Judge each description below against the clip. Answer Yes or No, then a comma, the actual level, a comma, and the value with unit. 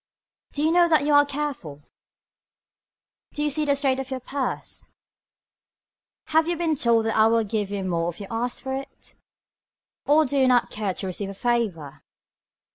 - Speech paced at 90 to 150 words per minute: No, average, 185 wpm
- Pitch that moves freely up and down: Yes, wide, 6.0 semitones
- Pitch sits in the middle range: No, very high, 255 Hz